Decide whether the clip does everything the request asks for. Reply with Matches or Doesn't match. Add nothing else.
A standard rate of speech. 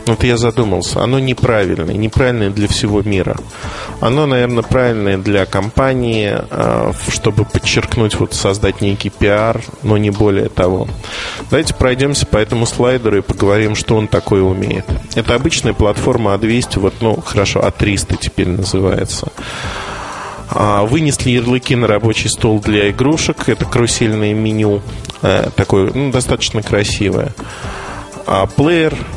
Matches